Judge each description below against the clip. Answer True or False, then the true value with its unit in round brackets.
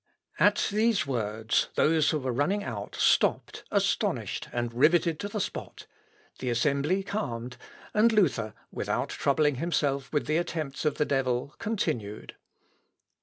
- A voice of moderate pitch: True (145 Hz)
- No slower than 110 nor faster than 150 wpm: True (140 wpm)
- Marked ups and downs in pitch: True (6.0 semitones)